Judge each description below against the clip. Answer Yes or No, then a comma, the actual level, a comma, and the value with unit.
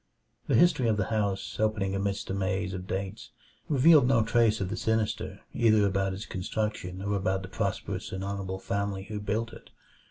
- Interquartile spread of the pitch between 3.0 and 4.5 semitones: No, narrow, 2.4 semitones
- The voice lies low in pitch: Yes, low, 100 Hz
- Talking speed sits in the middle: Yes, average, 185 wpm